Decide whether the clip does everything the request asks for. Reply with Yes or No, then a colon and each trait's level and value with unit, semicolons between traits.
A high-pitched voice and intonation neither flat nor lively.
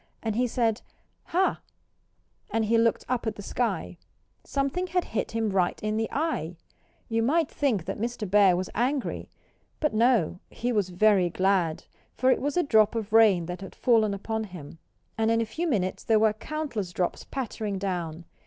Yes: high, 220 Hz; average, 4.1 semitones